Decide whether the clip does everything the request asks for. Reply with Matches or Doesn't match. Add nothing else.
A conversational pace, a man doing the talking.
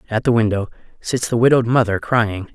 Matches